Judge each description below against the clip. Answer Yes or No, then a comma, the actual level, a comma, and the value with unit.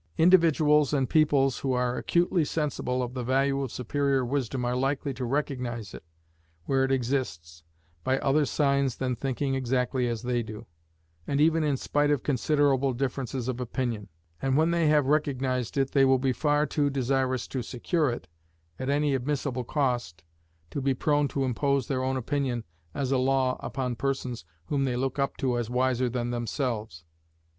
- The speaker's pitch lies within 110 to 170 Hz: Yes, low, 135 Hz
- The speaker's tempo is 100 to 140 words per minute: No, average, 175 wpm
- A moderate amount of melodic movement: No, narrow, 2.2 semitones